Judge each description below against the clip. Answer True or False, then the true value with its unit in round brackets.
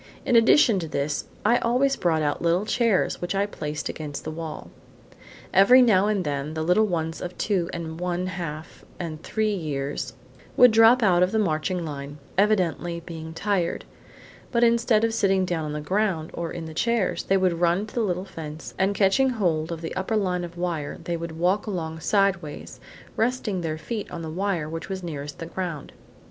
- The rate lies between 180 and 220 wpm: True (195 wpm)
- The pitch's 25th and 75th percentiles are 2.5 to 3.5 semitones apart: False (4.3 semitones)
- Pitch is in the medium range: True (180 Hz)